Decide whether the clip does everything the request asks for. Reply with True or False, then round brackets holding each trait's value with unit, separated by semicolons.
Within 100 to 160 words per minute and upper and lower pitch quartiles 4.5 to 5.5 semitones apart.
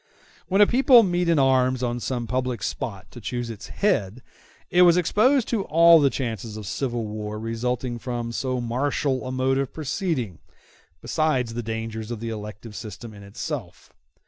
False (170 wpm; 5.0 semitones)